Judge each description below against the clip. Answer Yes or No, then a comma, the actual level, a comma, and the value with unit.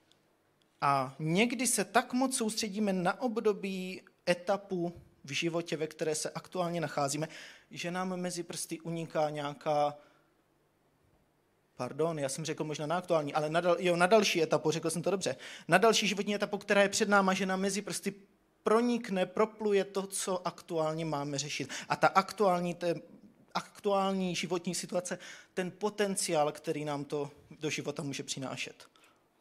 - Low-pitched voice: No, medium, 175 Hz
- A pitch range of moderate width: Yes, average, 4.1 semitones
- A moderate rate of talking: Yes, average, 155 wpm